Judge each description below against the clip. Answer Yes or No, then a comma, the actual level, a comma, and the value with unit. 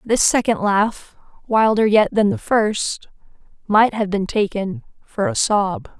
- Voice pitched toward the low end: No, high, 215 Hz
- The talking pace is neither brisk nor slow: Yes, average, 150 wpm